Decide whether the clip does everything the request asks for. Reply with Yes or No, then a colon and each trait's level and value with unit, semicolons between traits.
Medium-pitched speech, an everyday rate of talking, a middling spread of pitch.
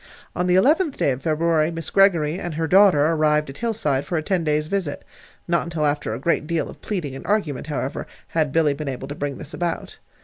No: medium, 155 Hz; fast, 225 wpm; average, 3.3 semitones